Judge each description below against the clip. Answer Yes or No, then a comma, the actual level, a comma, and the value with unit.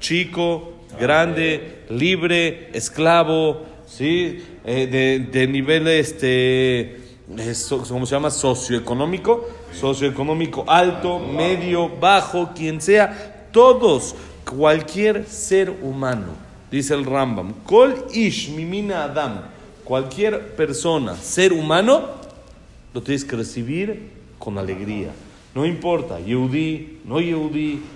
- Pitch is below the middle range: No, medium, 155 Hz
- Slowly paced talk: Yes, slow, 100 wpm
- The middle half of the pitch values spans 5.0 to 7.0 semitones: Yes, average, 5.3 semitones